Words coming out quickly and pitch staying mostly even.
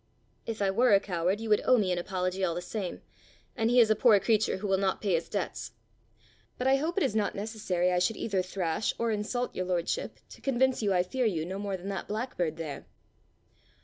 No: fast, 230 wpm; average, 3.7 semitones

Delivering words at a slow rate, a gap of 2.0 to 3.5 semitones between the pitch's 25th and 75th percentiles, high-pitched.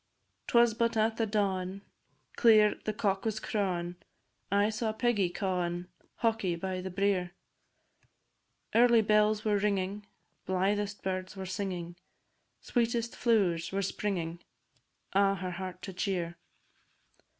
Yes: slow, 120 wpm; average, 2.7 semitones; high, 200 Hz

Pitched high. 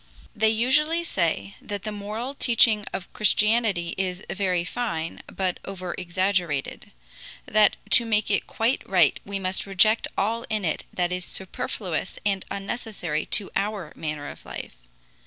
Yes: high, 195 Hz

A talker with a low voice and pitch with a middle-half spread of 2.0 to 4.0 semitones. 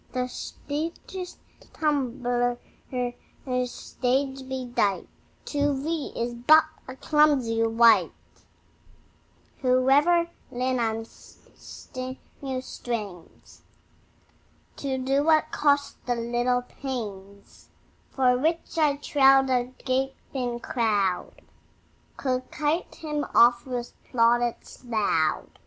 No: very high, 255 Hz; average, 2.9 semitones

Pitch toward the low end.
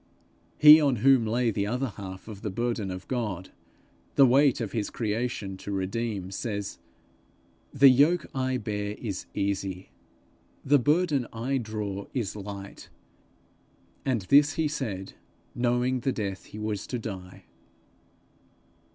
Yes: low, 115 Hz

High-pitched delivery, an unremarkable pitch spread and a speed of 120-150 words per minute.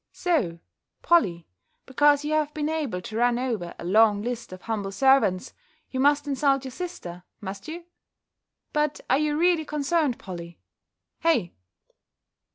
No: very high, 265 Hz; wide, 7.0 semitones; average, 145 wpm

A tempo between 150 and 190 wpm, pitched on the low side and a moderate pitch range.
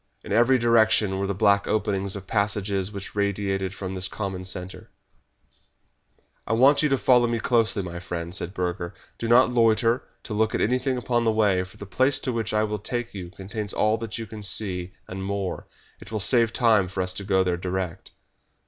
No: average, 200 wpm; low, 100 Hz; average, 3.3 semitones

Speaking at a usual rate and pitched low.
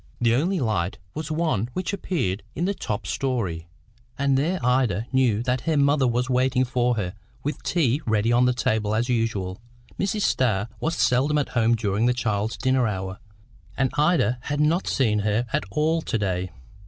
Yes: average, 180 wpm; low, 125 Hz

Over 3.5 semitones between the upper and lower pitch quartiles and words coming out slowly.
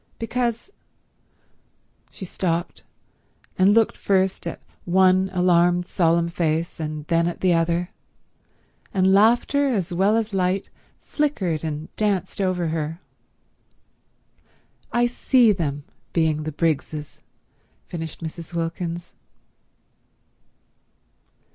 No: average, 3.0 semitones; slow, 100 wpm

